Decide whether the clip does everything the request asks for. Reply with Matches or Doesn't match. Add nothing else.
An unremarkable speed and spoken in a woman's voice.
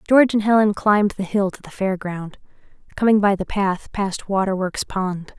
Matches